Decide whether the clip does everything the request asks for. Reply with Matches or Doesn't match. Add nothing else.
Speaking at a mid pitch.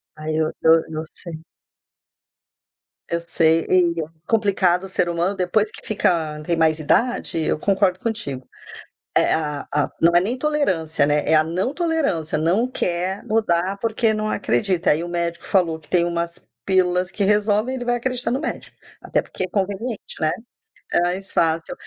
Matches